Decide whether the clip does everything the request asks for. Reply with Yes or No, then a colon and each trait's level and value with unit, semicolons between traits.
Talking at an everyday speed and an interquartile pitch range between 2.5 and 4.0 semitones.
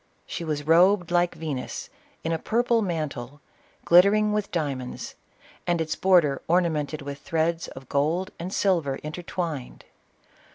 No: slow, 130 wpm; average, 3.5 semitones